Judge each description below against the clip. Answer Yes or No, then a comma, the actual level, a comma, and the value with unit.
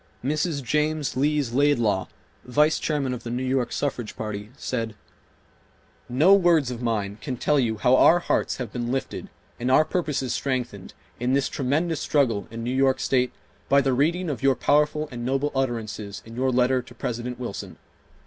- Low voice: Yes, low, 130 Hz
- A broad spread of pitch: No, average, 3.5 semitones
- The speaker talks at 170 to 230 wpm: Yes, average, 175 wpm